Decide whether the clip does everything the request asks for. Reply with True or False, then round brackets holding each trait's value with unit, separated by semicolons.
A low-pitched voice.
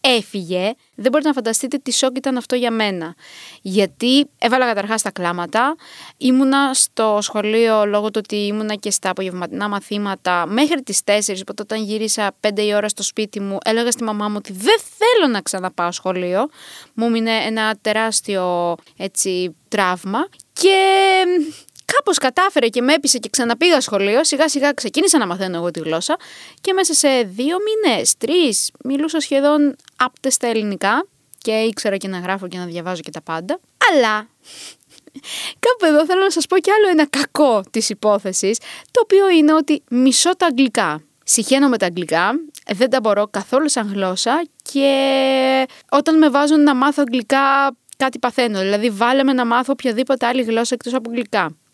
False (240 Hz)